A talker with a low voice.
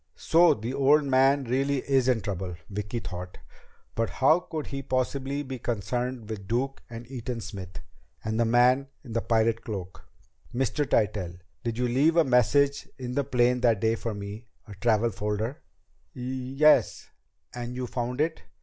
Yes: low, 120 Hz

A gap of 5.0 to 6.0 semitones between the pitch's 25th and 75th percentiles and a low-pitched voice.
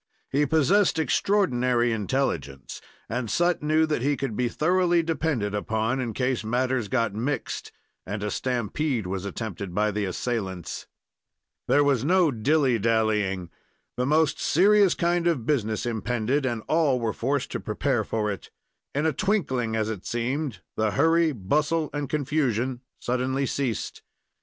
Yes: wide, 5.5 semitones; low, 125 Hz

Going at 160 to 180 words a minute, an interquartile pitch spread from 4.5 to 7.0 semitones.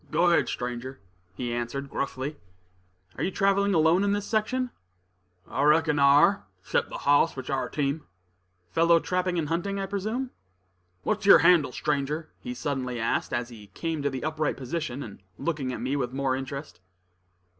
Yes: average, 175 wpm; average, 5.3 semitones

